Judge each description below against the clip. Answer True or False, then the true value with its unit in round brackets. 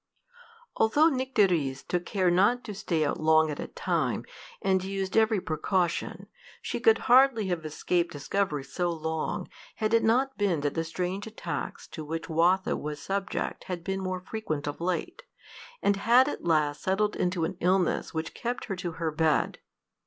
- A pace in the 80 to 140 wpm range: False (170 wpm)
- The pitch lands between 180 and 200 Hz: True (185 Hz)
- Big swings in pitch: False (4.5 semitones)